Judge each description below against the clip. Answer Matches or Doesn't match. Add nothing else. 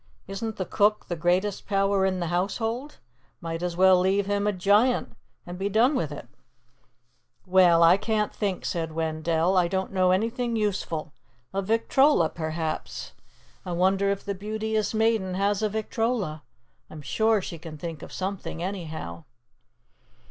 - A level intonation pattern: Doesn't match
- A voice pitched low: Doesn't match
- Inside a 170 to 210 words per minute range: Doesn't match